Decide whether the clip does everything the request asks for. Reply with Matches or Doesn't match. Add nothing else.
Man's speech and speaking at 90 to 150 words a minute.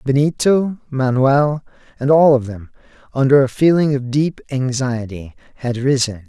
Matches